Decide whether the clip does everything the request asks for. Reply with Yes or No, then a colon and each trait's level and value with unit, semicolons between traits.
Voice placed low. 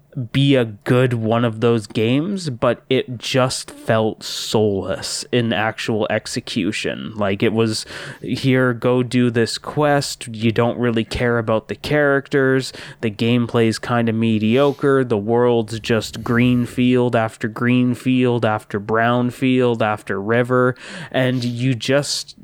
Yes: low, 120 Hz